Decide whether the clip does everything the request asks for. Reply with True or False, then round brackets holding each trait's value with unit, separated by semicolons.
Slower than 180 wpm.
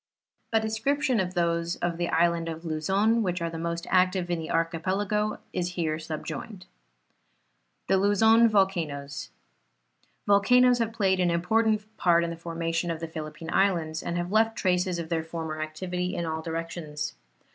True (165 wpm)